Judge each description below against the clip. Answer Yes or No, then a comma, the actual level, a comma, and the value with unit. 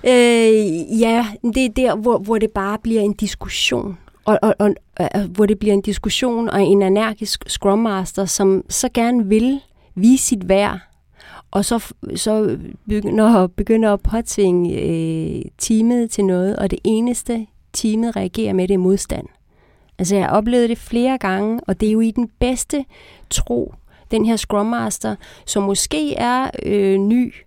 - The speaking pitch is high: Yes, high, 215 Hz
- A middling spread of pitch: Yes, average, 3.0 semitones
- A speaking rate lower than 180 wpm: Yes, average, 160 wpm